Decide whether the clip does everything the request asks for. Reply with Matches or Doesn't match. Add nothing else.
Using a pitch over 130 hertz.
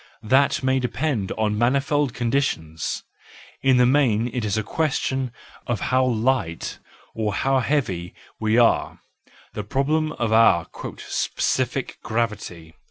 Doesn't match